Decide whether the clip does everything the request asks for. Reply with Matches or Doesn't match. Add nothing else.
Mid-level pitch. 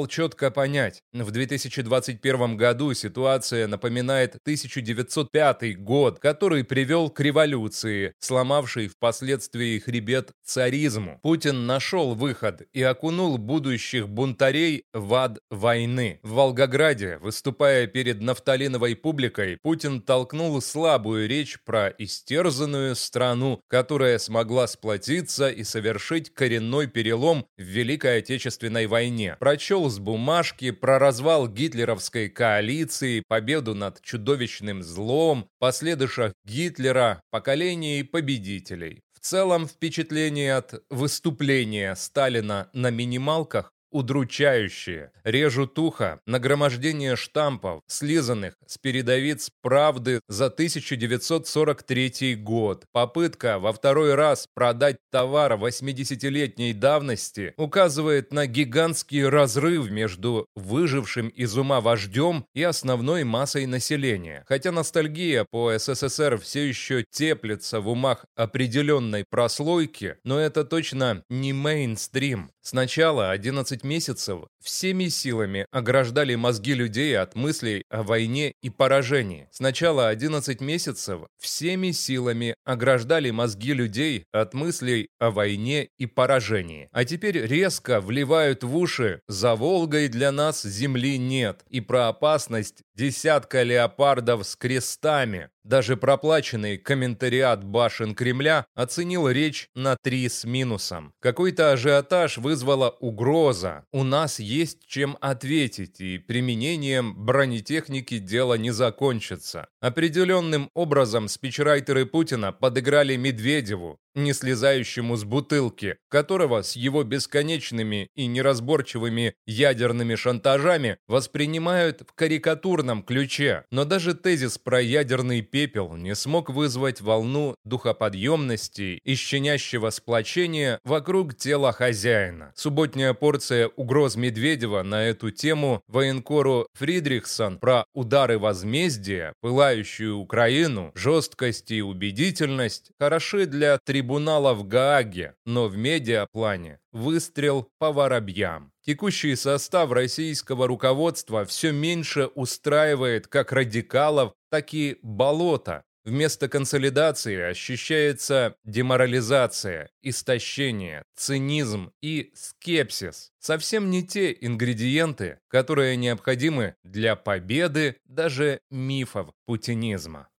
Doesn't match